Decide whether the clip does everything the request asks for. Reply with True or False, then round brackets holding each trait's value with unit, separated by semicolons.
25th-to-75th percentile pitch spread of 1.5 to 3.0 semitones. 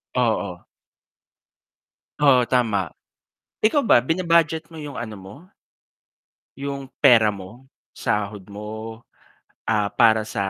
False (5.1 semitones)